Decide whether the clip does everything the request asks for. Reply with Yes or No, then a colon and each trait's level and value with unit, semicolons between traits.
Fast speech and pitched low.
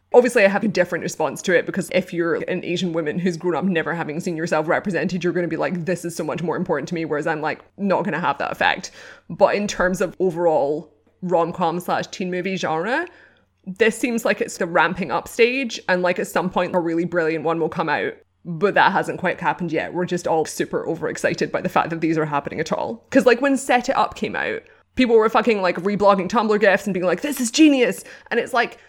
No: fast, 245 wpm; medium, 180 Hz